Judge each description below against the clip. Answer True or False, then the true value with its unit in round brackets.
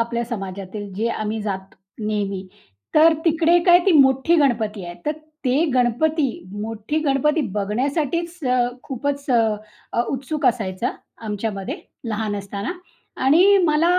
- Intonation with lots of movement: True (6.3 semitones)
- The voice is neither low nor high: False (235 Hz)